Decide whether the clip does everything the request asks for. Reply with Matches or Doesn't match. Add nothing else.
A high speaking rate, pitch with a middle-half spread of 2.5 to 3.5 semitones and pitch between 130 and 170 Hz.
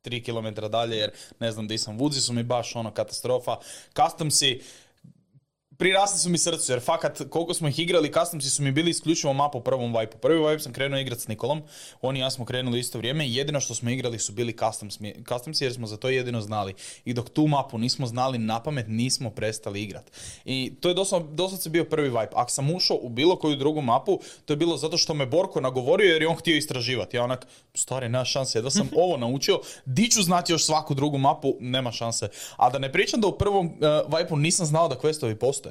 Doesn't match